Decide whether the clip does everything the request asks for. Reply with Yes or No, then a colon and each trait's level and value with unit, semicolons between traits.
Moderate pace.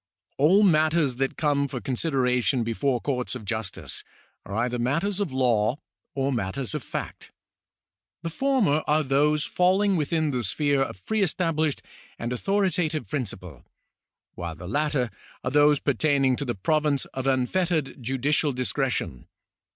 Yes: average, 145 wpm